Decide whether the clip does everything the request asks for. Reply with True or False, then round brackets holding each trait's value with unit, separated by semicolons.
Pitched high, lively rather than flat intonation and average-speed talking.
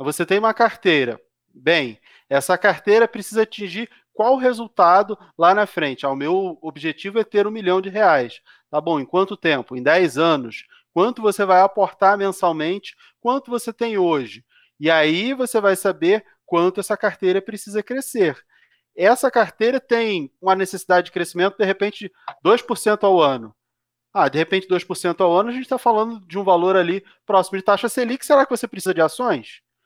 False (195 Hz; 4.2 semitones; 175 wpm)